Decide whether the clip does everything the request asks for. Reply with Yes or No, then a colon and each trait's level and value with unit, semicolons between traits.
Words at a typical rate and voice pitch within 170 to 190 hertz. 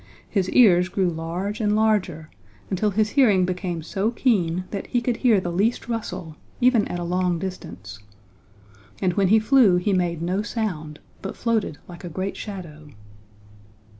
Yes: average, 165 wpm; medium, 185 Hz